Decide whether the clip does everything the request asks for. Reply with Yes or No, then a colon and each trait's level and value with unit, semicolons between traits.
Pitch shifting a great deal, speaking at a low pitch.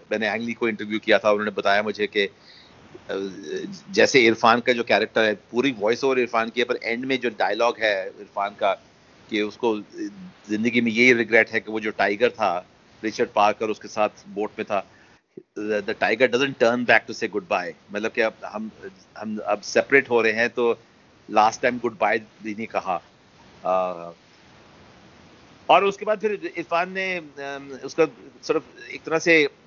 No: average, 4.1 semitones; low, 115 Hz